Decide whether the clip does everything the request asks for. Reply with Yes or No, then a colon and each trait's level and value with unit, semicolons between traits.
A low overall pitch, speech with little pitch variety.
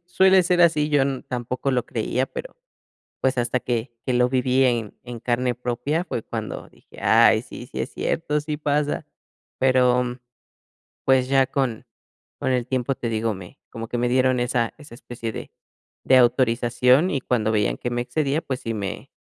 Yes: low, 125 Hz; narrow, 2.2 semitones